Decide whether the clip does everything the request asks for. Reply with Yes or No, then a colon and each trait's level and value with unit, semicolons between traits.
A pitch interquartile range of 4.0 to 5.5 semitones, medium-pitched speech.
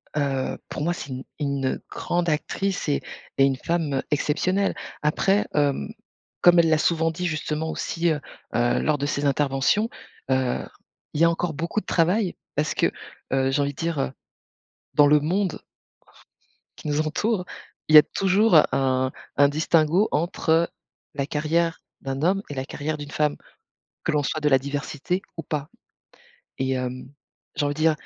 No: average, 3.2 semitones; medium, 150 Hz